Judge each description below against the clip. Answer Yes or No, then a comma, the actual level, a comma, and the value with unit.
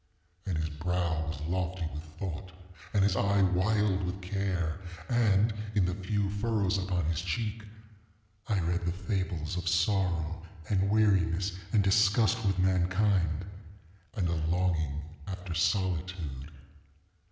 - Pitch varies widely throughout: No, average, 2.7 semitones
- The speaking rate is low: Yes, slow, 130 wpm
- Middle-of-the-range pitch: No, very low, 95 Hz